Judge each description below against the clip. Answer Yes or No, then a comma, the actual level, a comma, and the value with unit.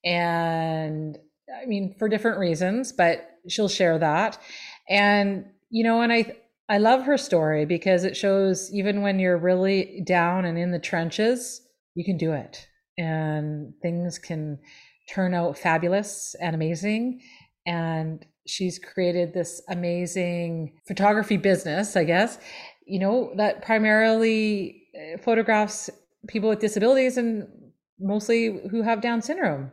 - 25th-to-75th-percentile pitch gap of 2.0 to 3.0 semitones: No, average, 4.2 semitones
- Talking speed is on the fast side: No, slow, 135 wpm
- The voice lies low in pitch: No, high, 190 Hz